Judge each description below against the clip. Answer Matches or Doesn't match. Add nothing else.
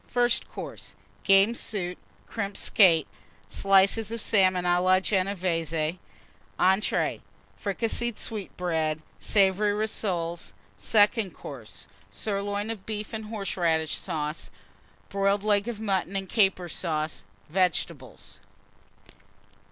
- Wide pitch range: Doesn't match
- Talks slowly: Matches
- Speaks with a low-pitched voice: Doesn't match